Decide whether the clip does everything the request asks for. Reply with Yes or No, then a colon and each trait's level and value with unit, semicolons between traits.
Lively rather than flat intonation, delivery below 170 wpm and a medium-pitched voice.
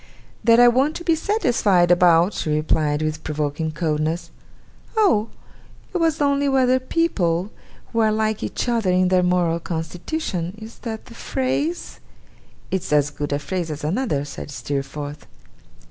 Yes: wide, 8.0 semitones; average, 150 wpm; medium, 180 Hz